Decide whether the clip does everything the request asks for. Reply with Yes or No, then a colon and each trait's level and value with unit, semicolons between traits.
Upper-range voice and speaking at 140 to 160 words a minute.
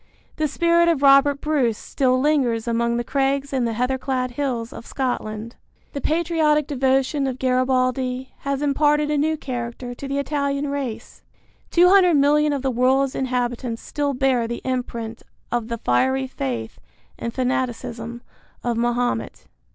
Yes: very high, 260 Hz; average, 150 wpm